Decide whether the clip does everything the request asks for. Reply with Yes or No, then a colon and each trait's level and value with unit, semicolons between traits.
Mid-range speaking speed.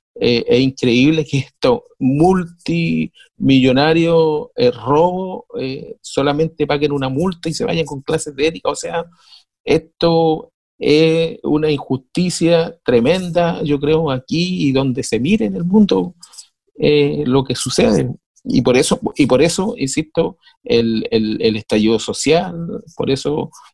Yes: average, 140 wpm